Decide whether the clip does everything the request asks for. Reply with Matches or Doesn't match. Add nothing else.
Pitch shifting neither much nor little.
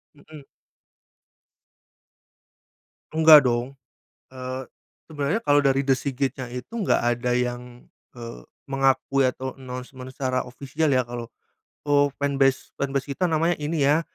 Doesn't match